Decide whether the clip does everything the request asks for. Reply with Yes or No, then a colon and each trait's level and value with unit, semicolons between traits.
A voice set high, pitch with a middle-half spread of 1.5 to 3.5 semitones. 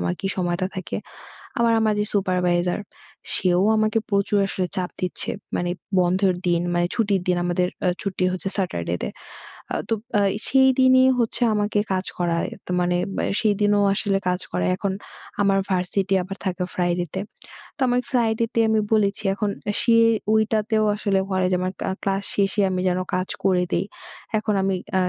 Yes: high, 195 Hz; average, 2.9 semitones